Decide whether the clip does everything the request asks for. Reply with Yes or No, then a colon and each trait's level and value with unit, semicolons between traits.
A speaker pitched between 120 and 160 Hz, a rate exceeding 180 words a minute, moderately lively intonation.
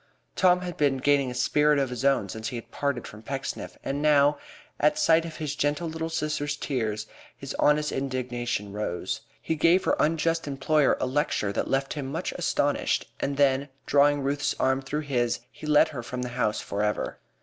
Yes: medium, 140 Hz; average, 195 wpm; average, 3.1 semitones